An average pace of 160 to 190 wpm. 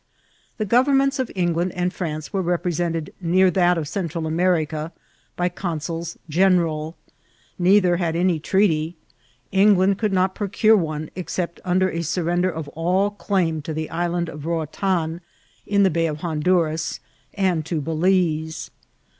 No: average, 150 wpm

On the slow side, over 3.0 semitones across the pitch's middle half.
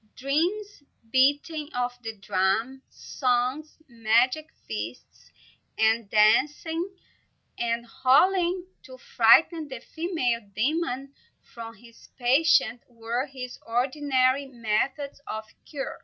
Yes: slow, 95 wpm; average, 4.6 semitones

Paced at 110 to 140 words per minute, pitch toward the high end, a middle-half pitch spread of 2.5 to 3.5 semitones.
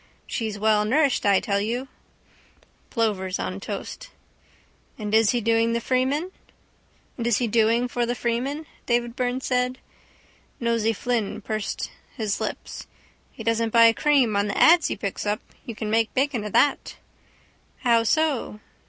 Yes: slow, 135 wpm; high, 230 Hz; average, 2.8 semitones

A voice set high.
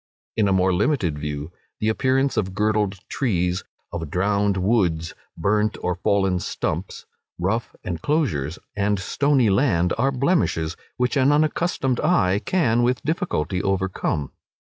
No: low, 100 Hz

